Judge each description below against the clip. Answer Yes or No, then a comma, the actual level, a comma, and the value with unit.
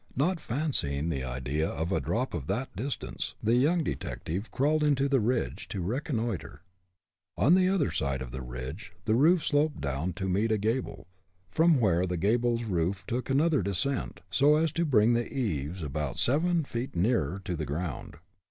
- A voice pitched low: Yes, low, 110 Hz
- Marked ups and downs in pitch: Yes, wide, 8.8 semitones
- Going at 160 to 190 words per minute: Yes, average, 180 wpm